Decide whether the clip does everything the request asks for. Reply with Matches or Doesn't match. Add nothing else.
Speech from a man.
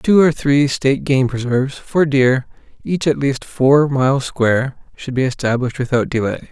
Matches